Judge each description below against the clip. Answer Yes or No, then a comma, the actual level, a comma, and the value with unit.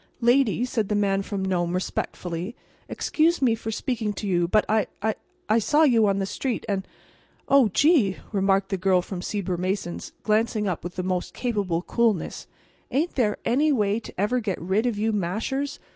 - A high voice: Yes, high, 210 Hz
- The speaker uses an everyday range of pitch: Yes, average, 3.8 semitones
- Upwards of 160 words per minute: Yes, average, 175 wpm